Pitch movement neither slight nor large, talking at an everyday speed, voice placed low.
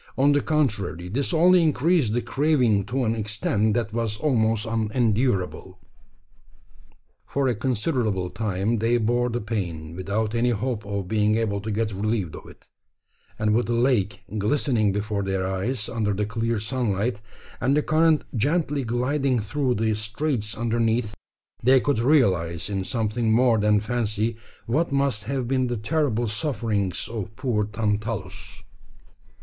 Yes: average, 3.4 semitones; average, 150 wpm; low, 115 Hz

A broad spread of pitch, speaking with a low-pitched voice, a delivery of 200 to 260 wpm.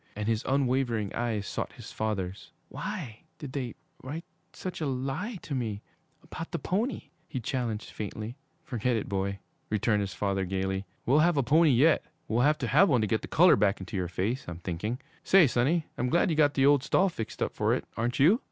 Yes: wide, 5.9 semitones; low, 120 Hz; fast, 205 wpm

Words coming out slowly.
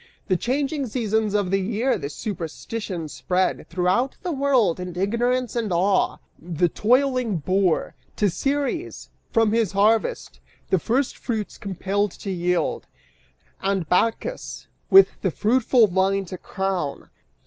Yes: slow, 130 wpm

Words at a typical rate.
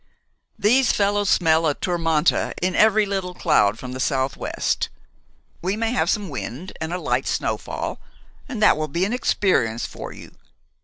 Yes: average, 160 wpm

